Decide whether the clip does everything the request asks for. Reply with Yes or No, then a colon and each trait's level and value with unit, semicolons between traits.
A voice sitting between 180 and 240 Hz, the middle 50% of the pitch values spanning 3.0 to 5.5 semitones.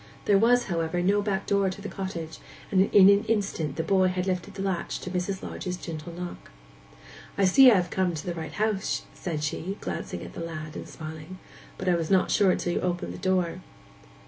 No: medium, 185 Hz; narrow, 2.6 semitones